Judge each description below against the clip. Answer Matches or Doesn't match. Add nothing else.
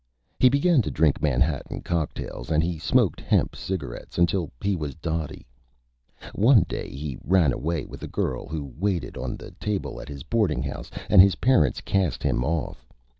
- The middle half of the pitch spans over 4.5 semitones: Matches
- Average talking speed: Matches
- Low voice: Matches